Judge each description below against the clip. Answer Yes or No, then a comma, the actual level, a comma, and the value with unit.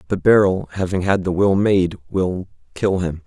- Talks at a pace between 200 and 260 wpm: No, average, 165 wpm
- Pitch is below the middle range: Yes, very low, 95 Hz